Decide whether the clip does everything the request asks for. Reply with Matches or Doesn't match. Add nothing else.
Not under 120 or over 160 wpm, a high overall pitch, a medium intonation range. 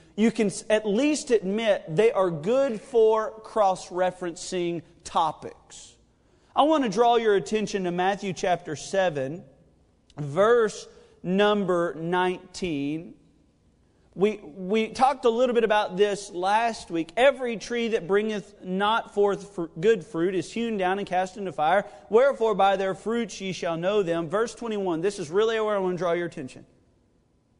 Matches